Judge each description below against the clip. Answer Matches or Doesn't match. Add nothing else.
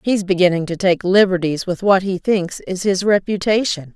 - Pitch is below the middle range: Doesn't match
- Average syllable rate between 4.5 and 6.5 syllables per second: Matches